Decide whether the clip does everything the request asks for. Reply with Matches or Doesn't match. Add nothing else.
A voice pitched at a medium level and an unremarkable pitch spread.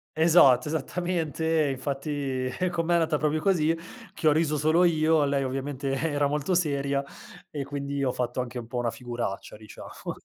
Matches